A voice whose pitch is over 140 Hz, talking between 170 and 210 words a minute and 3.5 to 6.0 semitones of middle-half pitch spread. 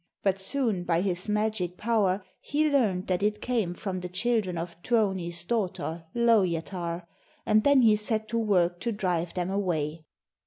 No: high, 190 Hz; average, 160 wpm; average, 3.8 semitones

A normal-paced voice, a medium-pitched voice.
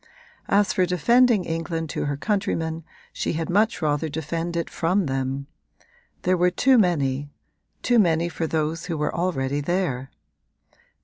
Yes: average, 145 wpm; medium, 165 Hz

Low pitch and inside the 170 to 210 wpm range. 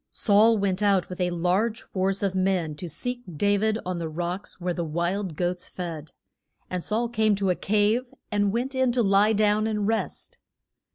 No: high, 200 Hz; average, 190 wpm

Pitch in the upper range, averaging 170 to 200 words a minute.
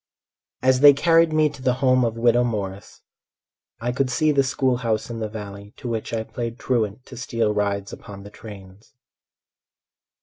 No: low, 115 Hz; average, 175 wpm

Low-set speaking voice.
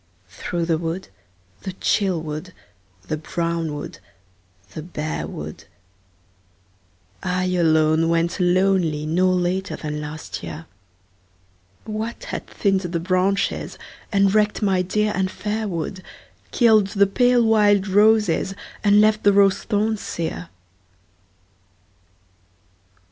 No: medium, 185 Hz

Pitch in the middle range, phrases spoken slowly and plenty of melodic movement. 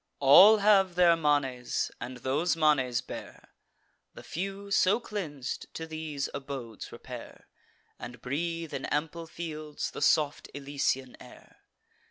No: medium, 150 Hz; slow, 125 wpm; average, 4.0 semitones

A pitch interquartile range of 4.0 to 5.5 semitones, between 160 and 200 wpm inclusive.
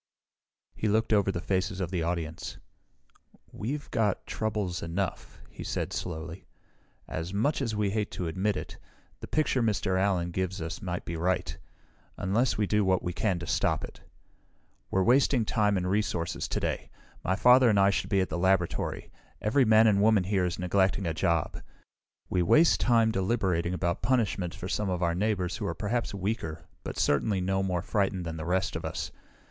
No: average, 3.2 semitones; average, 185 wpm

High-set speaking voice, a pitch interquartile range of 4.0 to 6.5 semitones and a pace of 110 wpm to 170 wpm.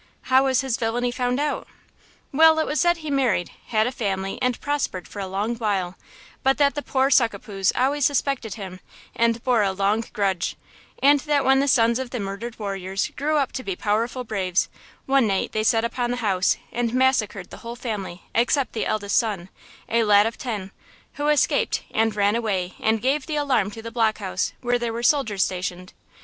No: high, 230 Hz; average, 4.6 semitones; average, 200 wpm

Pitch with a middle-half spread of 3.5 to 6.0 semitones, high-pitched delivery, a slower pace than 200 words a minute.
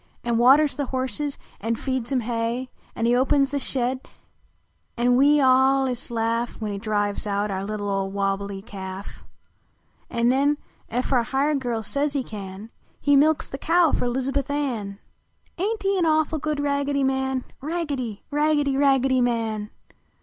Yes: average, 4.0 semitones; very high, 255 Hz; average, 165 wpm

